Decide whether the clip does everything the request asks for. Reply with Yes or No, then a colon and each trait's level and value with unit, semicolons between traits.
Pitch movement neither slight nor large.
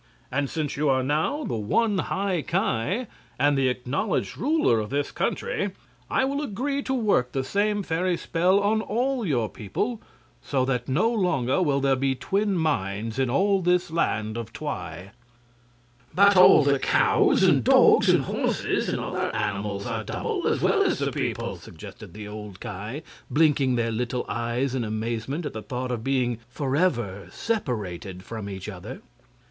No: wide, 8.5 semitones